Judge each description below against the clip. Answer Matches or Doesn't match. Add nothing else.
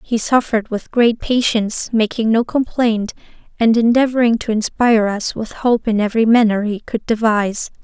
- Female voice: Matches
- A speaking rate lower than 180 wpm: Matches